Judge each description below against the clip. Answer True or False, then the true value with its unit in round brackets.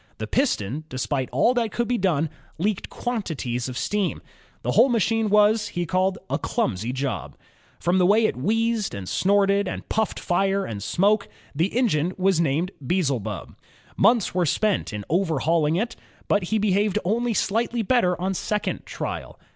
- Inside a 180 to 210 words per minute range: False (155 wpm)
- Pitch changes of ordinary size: False (5.7 semitones)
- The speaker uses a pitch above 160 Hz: True (190 Hz)